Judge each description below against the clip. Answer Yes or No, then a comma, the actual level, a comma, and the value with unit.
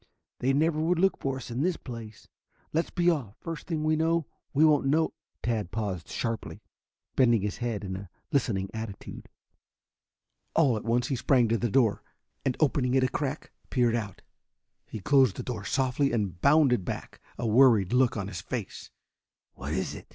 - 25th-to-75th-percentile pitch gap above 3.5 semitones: Yes, average, 4.9 semitones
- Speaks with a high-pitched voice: No, low, 125 Hz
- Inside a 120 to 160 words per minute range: No, average, 185 wpm